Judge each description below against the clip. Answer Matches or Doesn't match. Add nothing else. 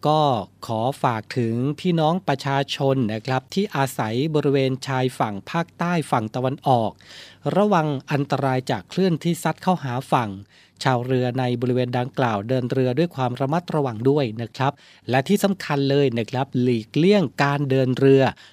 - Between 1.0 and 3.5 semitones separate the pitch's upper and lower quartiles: Matches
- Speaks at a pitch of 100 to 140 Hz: Matches